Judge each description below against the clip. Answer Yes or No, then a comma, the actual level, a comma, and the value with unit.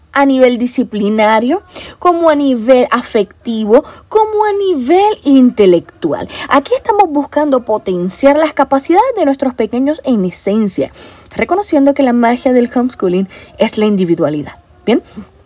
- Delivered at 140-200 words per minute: No, slow, 125 wpm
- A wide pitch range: Yes, wide, 5.8 semitones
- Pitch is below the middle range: No, very high, 255 Hz